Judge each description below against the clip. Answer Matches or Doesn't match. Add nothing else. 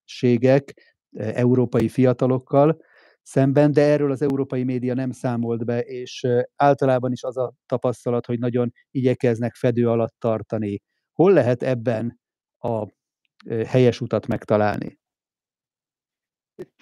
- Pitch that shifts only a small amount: Matches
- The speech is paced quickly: Doesn't match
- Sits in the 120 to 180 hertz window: Matches